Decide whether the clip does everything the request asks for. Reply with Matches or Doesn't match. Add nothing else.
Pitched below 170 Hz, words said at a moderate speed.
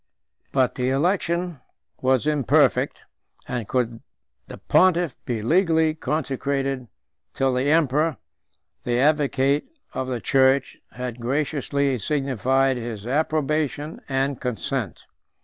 Doesn't match